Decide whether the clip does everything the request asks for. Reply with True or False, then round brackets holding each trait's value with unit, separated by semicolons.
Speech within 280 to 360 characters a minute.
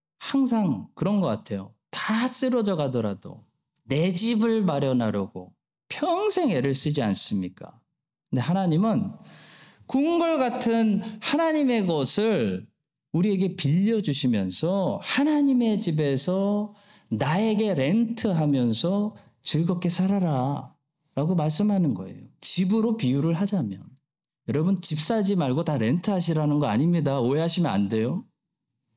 False (265 characters per minute)